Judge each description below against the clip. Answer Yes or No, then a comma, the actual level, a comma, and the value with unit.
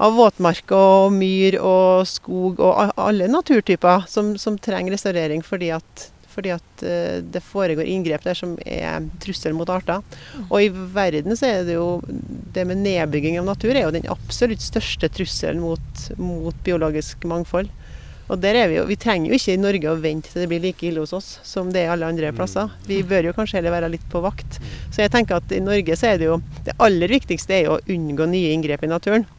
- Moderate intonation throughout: Yes, average, 3.0 semitones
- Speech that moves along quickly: Yes, fast, 215 wpm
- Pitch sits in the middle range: Yes, medium, 180 Hz